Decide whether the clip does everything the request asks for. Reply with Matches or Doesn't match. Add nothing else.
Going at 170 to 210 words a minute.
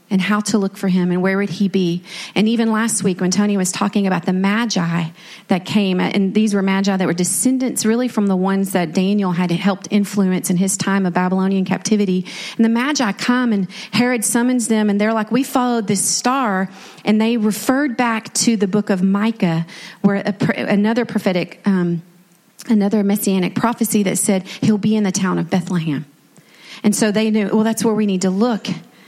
Matches